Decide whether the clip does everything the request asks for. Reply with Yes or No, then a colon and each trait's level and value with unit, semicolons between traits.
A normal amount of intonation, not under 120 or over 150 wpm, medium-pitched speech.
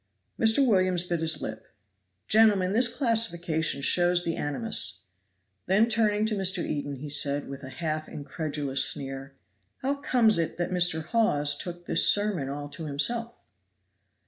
No: wide, 6.8 semitones; average, 145 wpm; medium, 175 Hz